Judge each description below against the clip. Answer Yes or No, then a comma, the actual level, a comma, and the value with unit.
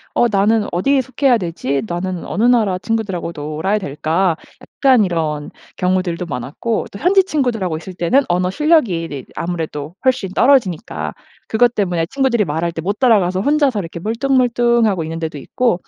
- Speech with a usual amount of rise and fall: No, wide, 6.2 semitones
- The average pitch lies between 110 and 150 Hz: No, high, 190 Hz